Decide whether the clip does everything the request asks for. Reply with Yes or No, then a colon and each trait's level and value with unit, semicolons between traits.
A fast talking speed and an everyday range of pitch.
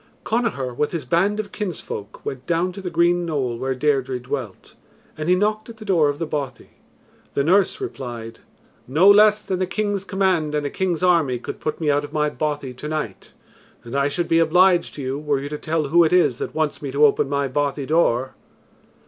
Yes: fast, 215 wpm; average, 4.7 semitones